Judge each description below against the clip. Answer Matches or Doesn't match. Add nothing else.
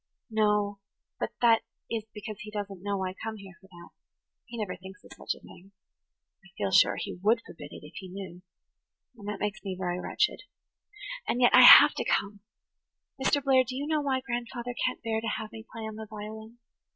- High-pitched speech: Matches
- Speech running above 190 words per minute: Matches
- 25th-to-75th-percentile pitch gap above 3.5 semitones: Doesn't match